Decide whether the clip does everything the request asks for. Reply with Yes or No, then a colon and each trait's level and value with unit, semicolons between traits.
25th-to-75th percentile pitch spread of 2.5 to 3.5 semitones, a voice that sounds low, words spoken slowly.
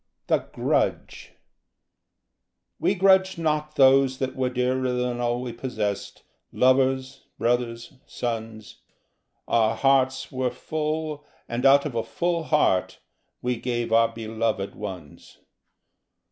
Yes: average, 2.9 semitones; low, 125 Hz; slow, 115 wpm